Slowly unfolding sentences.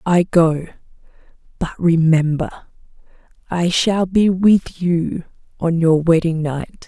Yes: slow, 115 wpm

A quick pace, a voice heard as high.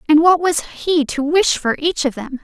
Yes: fast, 245 wpm; very high, 305 Hz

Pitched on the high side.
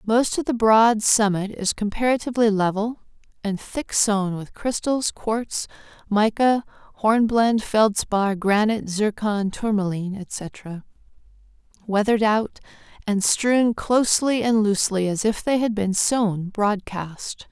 Yes: high, 215 Hz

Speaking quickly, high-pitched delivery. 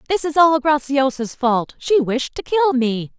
No: average, 190 wpm; very high, 275 Hz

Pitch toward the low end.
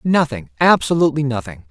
Yes: low, 130 Hz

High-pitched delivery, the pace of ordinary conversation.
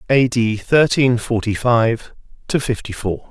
No: low, 120 Hz; average, 145 wpm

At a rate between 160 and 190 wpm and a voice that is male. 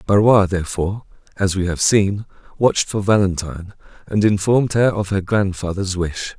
No: average, 150 wpm; male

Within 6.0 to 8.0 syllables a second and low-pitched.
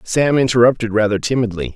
Yes: 6.1 syllables/s; low, 115 Hz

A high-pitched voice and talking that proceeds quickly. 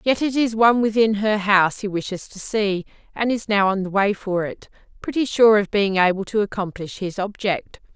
Yes: high, 205 Hz; fast, 210 wpm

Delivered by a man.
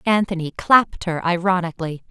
No: female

